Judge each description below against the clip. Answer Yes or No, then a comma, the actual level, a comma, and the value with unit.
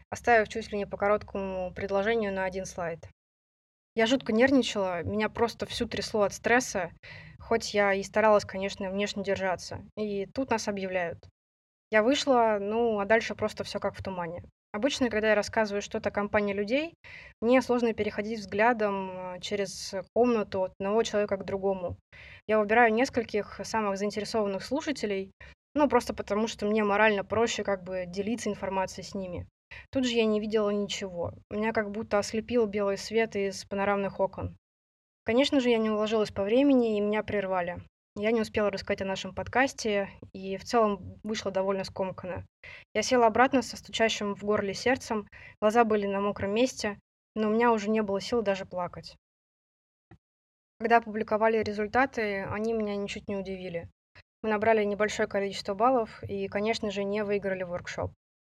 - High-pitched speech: Yes, high, 210 Hz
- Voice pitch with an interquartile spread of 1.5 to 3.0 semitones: Yes, narrow, 2.5 semitones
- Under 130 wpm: No, fast, 160 wpm